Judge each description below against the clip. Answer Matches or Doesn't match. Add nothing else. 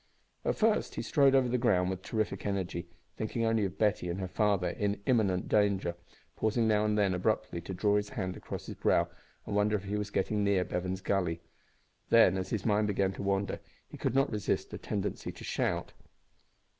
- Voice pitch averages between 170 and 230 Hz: Doesn't match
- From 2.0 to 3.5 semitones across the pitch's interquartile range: Matches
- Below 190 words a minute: Doesn't match